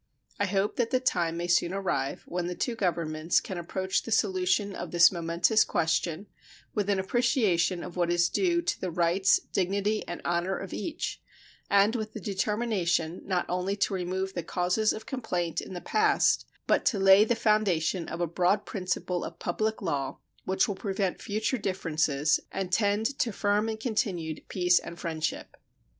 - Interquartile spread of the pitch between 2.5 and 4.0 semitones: Yes, average, 3.4 semitones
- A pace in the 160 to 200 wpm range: Yes, average, 175 wpm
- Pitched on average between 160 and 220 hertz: Yes, high, 190 Hz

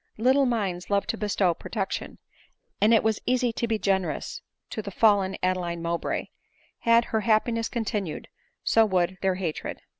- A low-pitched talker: No, high, 210 Hz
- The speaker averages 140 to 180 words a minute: Yes, average, 155 wpm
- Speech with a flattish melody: No, average, 3.6 semitones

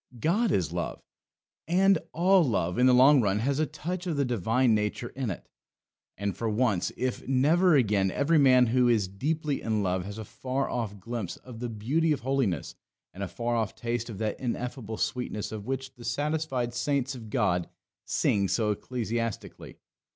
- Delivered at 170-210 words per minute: Yes, average, 180 wpm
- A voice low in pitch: Yes, low, 120 Hz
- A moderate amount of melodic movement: Yes, average, 4.6 semitones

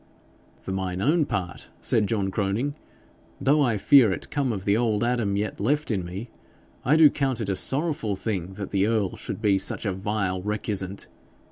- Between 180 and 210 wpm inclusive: Yes, average, 190 wpm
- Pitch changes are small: No, average, 4.1 semitones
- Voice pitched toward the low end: Yes, low, 105 Hz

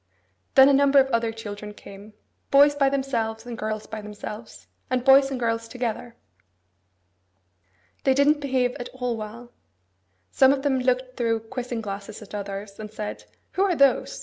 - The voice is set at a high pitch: Yes, high, 240 Hz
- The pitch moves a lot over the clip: No, average, 3.7 semitones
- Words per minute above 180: No, average, 165 wpm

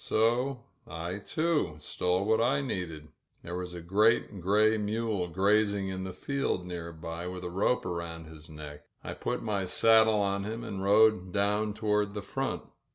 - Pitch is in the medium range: No, low, 100 Hz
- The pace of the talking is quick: No, average, 170 wpm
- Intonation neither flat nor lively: Yes, average, 3.6 semitones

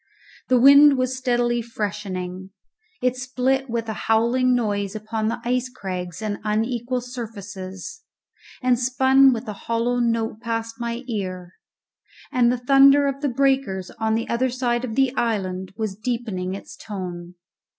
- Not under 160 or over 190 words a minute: No, average, 150 wpm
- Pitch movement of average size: Yes, average, 3.5 semitones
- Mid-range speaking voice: No, high, 235 Hz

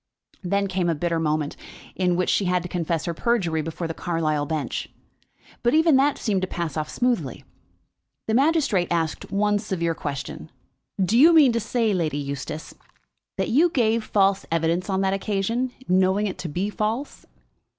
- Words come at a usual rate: Yes, average, 170 wpm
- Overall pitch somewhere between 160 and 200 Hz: Yes, high, 190 Hz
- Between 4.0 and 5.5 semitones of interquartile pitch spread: Yes, average, 5.1 semitones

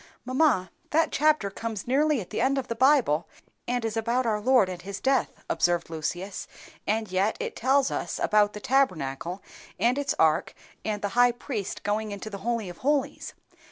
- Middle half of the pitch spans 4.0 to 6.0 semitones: Yes, average, 5.0 semitones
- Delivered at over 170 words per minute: Yes, average, 185 wpm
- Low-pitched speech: No, high, 220 Hz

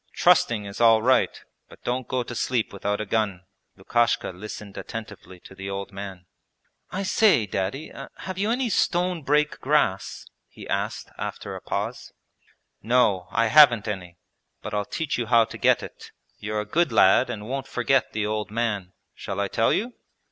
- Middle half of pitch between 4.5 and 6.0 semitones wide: Yes, average, 4.9 semitones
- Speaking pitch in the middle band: No, low, 110 Hz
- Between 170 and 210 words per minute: Yes, average, 175 wpm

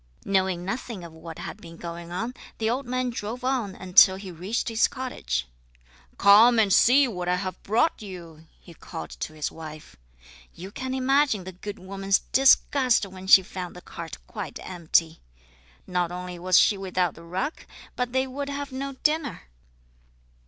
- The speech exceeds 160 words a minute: Yes, average, 170 wpm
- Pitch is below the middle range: No, high, 195 Hz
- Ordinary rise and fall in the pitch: No, wide, 5.9 semitones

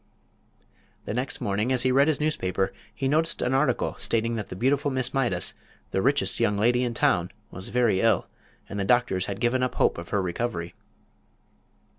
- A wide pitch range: No, average, 4.9 semitones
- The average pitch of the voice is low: Yes, low, 120 Hz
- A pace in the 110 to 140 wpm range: No, average, 185 wpm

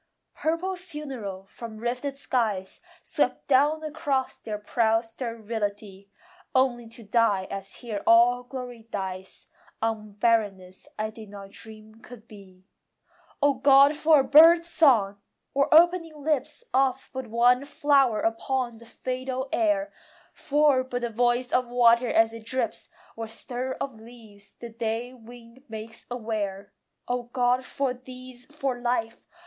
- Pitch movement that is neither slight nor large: Yes, average, 3.2 semitones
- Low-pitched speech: No, high, 240 Hz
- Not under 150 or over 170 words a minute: No, average, 140 wpm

